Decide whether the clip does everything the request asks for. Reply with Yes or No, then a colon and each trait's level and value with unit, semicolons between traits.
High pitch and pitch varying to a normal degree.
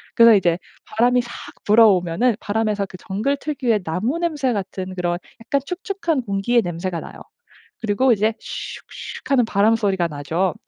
Yes: high, 215 Hz; average, 4.8 semitones